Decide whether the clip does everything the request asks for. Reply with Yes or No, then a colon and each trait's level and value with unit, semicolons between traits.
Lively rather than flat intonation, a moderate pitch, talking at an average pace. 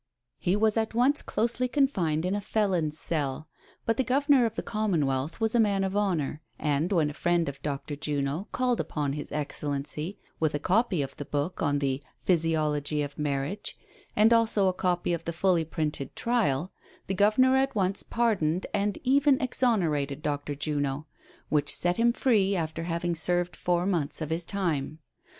Yes: wide, 6.2 semitones; medium, 175 Hz; average, 175 wpm